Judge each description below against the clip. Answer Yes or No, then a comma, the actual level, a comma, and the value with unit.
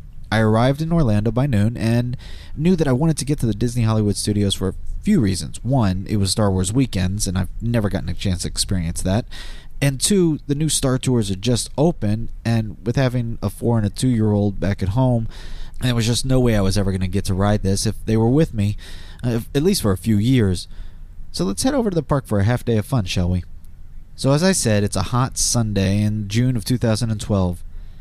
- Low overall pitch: Yes, low, 105 Hz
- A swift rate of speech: Yes, fast, 240 wpm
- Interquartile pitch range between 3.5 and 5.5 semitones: Yes, average, 4.8 semitones